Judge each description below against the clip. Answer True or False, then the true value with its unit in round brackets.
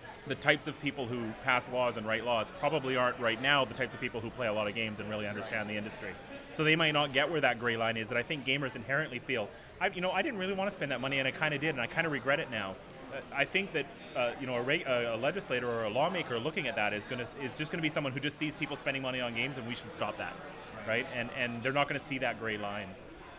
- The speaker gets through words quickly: True (300 wpm)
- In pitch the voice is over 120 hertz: True (130 Hz)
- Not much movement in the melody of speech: False (3.8 semitones)